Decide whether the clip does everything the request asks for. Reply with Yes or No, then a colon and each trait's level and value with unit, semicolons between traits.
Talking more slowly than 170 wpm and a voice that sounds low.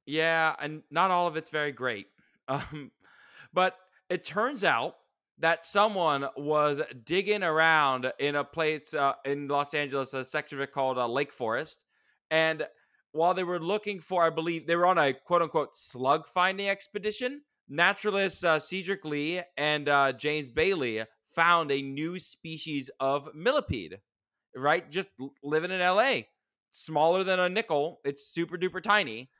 No: average, 155 wpm; medium, 160 Hz